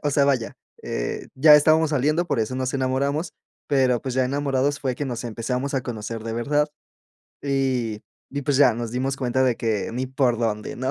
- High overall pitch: No, low, 130 Hz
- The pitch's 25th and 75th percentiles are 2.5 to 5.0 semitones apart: Yes, average, 2.9 semitones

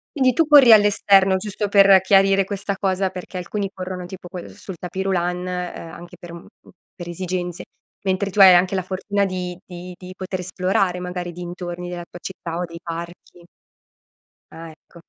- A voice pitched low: No, medium, 185 Hz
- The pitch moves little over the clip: Yes, narrow, 1.7 semitones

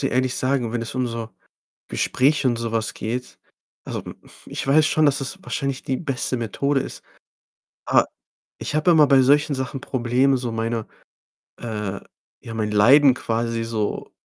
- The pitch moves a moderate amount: Yes, average, 3.2 semitones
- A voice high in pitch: No, low, 125 Hz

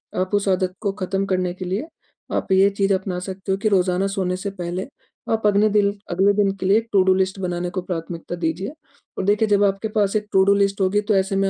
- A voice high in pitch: Yes, high, 195 Hz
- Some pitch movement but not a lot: No, narrow, 1.5 semitones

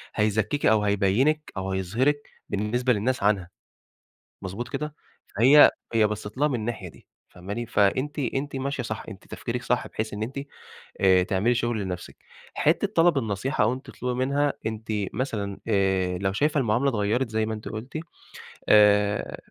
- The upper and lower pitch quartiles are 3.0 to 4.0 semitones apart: No, average, 4.5 semitones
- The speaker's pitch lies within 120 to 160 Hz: No, low, 110 Hz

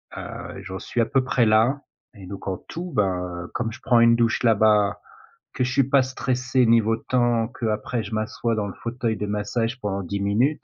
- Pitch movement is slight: No, average, 3.0 semitones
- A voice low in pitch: Yes, low, 115 Hz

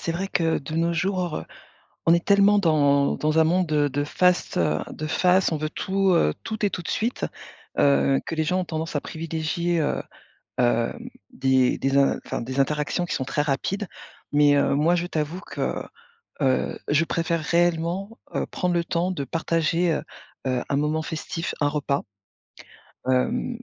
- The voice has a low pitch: No, medium, 160 Hz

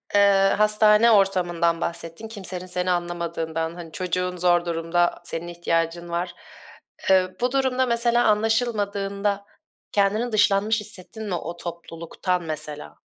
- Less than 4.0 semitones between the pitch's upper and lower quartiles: Yes, average, 3.6 semitones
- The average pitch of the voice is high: No, medium, 180 Hz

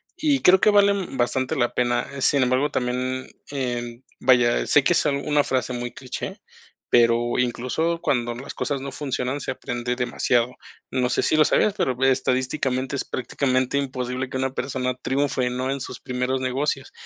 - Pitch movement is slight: Yes, narrow, 1.9 semitones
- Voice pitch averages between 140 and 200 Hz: No, low, 130 Hz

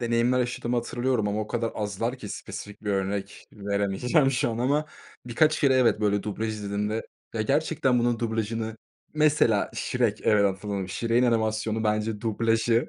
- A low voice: Yes, low, 115 Hz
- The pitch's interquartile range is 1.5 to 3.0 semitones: Yes, average, 2.7 semitones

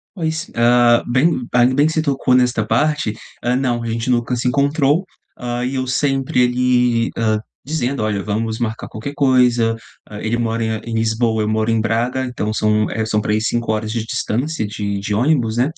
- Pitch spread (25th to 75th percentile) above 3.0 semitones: No, average, 2.7 semitones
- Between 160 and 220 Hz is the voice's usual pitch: No, low, 120 Hz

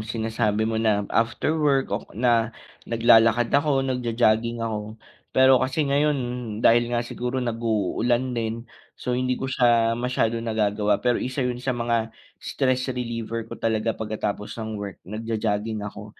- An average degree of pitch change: No, narrow, 2.1 semitones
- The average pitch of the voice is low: Yes, low, 115 Hz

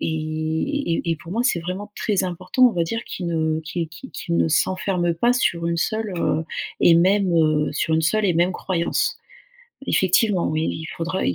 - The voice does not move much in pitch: No, average, 3.2 semitones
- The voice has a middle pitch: Yes, medium, 170 Hz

